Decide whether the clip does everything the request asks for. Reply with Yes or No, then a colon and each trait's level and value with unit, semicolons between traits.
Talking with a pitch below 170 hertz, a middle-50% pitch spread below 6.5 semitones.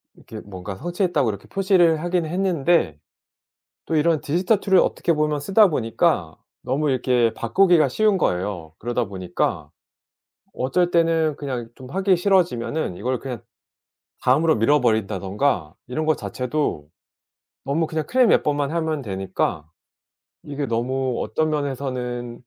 Yes: medium, 140 Hz; wide, 6.1 semitones